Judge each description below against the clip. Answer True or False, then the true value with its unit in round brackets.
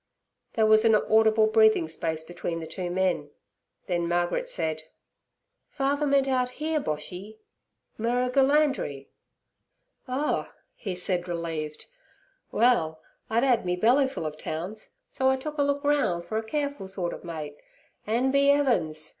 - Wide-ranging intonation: True (7.8 semitones)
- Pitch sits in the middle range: False (215 Hz)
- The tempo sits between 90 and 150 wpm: True (140 wpm)